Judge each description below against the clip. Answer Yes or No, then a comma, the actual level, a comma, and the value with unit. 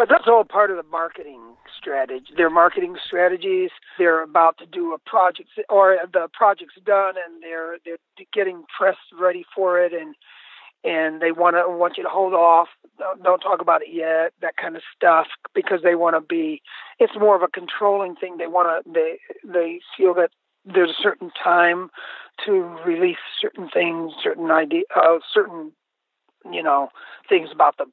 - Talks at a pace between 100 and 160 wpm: No, average, 175 wpm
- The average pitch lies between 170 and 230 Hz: Yes, medium, 185 Hz